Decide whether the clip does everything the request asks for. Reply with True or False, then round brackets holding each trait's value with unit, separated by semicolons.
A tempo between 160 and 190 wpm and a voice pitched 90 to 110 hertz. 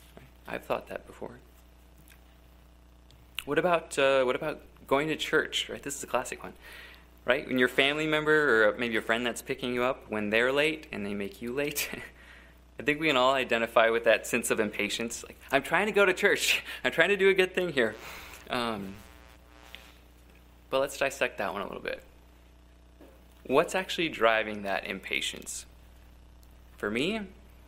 True (175 wpm; 105 Hz)